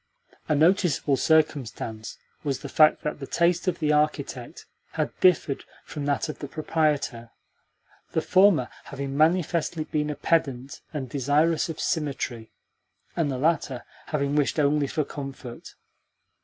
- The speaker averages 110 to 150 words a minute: Yes, average, 140 wpm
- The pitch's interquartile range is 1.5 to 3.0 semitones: Yes, narrow, 2.6 semitones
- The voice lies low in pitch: No, medium, 150 Hz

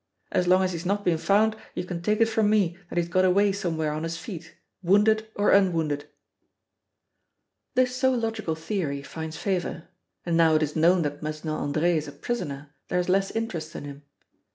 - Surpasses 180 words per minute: Yes, average, 195 wpm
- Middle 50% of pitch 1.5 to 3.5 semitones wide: No, average, 4.3 semitones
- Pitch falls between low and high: Yes, medium, 175 Hz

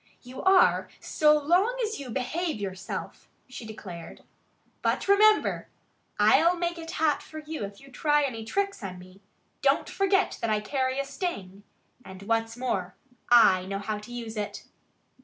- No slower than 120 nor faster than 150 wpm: No, average, 160 wpm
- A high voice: Yes, very high, 255 Hz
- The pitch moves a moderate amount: No, wide, 7.8 semitones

